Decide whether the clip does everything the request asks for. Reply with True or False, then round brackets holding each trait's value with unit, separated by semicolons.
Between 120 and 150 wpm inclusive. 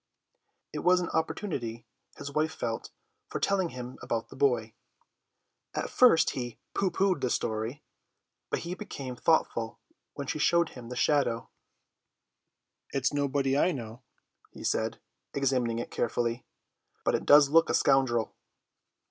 True (145 wpm)